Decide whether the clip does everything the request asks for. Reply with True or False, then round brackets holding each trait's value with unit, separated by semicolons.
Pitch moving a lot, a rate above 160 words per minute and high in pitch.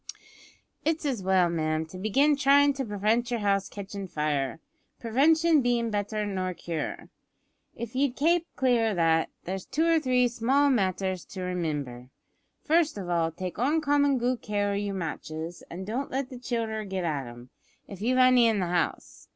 True (6.2 semitones; 175 wpm; 210 Hz)